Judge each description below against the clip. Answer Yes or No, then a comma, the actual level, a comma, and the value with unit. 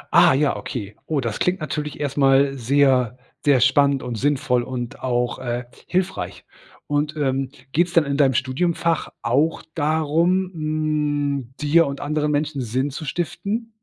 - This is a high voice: No, medium, 145 Hz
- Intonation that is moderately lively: Yes, average, 3.0 semitones